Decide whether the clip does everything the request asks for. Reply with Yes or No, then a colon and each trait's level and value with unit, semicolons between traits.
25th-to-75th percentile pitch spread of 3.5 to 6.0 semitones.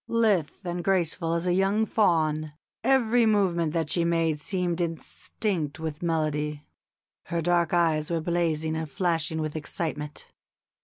No: narrow, 2.4 semitones